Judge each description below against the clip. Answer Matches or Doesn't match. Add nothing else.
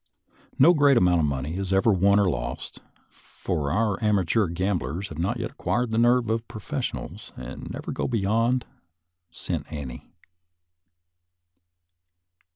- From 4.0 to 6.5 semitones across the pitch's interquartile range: Matches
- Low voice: Matches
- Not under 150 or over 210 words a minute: Doesn't match